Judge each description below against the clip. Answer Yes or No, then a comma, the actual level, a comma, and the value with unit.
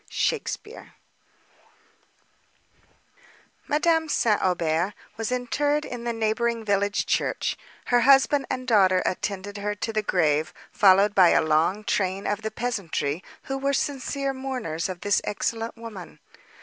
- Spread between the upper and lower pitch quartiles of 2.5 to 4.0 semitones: No, average, 4.9 semitones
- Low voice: No, high, 215 Hz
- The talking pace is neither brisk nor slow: No, slow, 130 wpm